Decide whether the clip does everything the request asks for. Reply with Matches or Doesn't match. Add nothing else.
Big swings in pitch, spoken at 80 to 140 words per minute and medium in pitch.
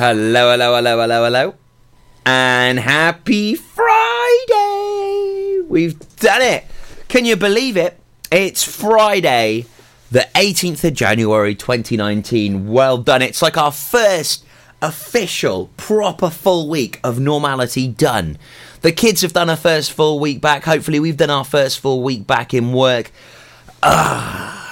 Matches